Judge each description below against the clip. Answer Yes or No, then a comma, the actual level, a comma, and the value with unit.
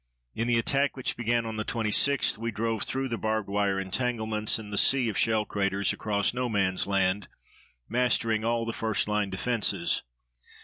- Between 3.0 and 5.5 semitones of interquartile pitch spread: No, narrow, 2.5 semitones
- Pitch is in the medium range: No, low, 110 Hz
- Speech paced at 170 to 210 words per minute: Yes, average, 175 wpm